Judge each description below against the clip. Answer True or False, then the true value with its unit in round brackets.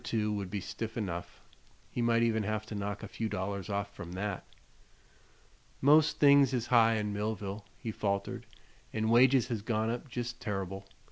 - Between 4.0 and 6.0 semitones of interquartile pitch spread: False (2.7 semitones)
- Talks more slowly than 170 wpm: False (175 wpm)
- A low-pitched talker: True (110 Hz)